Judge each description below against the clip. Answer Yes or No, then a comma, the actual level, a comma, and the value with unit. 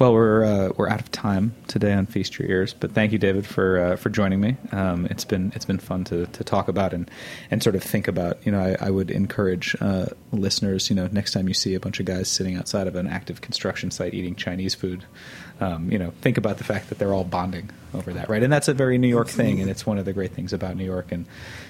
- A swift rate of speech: Yes, fast, 270 wpm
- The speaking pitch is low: Yes, very low, 95 Hz